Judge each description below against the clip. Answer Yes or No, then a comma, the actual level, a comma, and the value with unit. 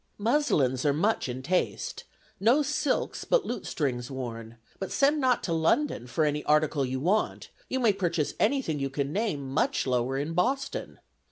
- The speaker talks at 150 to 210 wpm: Yes, average, 170 wpm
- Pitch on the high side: No, medium, 160 Hz